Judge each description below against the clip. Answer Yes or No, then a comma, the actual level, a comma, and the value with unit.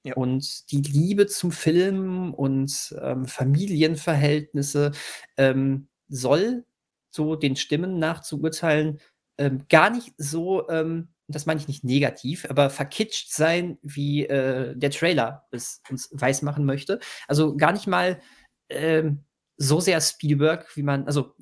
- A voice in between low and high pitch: Yes, medium, 150 Hz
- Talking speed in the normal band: Yes, average, 140 wpm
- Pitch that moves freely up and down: No, average, 2.7 semitones